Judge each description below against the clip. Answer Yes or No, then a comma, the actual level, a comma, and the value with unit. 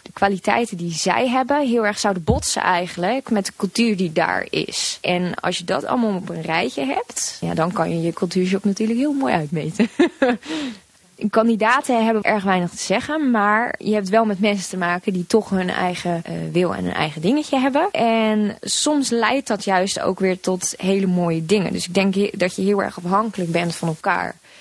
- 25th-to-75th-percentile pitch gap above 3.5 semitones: Yes, average, 3.9 semitones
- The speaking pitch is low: No, high, 200 Hz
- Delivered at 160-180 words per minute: No, fast, 200 wpm